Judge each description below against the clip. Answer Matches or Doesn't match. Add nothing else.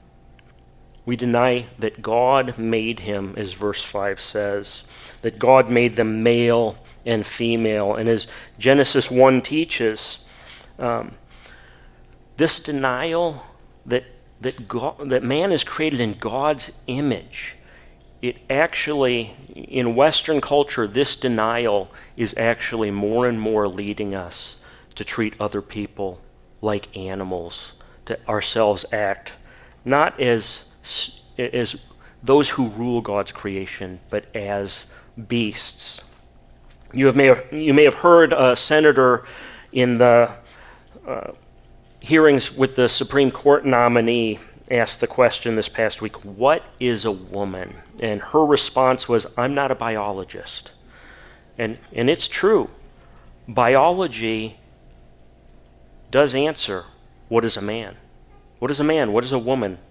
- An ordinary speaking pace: Doesn't match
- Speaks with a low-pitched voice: Matches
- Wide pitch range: Doesn't match